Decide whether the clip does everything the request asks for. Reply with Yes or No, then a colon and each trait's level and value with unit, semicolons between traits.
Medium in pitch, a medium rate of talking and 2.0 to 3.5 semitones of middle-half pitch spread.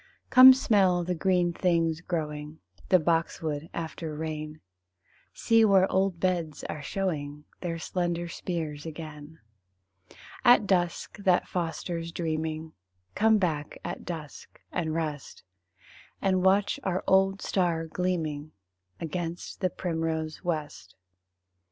No: medium, 170 Hz; slow, 115 wpm; average, 2.8 semitones